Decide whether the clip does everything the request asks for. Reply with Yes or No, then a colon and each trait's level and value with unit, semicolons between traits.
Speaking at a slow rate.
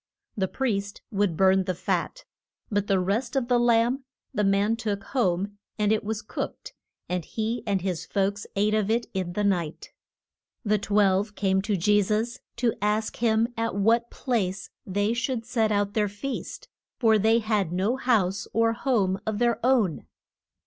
No: average, 170 wpm